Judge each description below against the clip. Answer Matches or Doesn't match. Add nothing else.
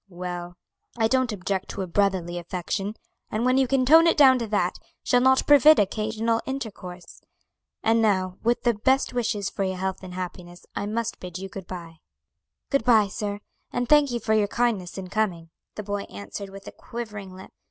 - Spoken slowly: Doesn't match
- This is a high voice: Matches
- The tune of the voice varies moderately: Matches